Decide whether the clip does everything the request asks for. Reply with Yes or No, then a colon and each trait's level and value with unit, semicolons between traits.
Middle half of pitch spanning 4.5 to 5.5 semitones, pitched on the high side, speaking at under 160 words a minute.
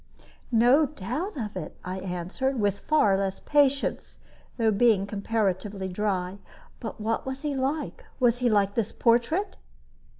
Yes: average, 5.2 semitones; high, 220 Hz; average, 140 wpm